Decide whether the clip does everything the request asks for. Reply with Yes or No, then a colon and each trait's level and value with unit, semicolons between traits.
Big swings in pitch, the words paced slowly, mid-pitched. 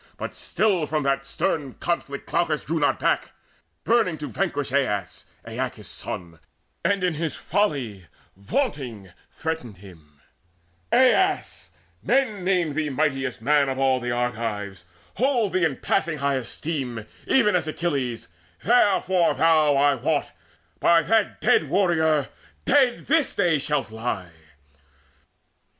Yes: wide, 6.1 semitones; slow, 130 wpm; medium, 150 Hz